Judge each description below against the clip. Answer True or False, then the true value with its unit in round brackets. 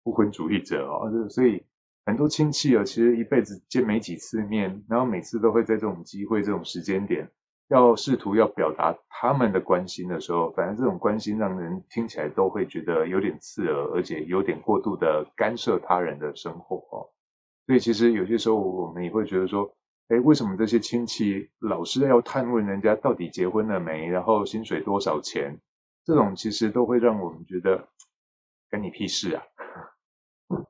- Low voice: True (110 Hz)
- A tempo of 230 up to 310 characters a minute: True (285 characters per minute)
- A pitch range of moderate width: True (3.4 semitones)